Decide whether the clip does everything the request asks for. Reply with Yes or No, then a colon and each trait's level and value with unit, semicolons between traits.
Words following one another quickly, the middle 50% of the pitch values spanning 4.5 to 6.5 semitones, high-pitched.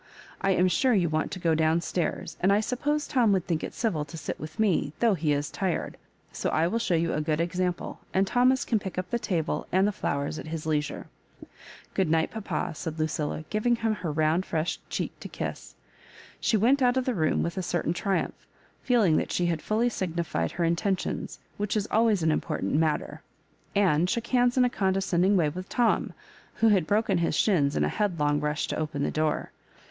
No: fast, 215 wpm; average, 5.2 semitones; medium, 180 Hz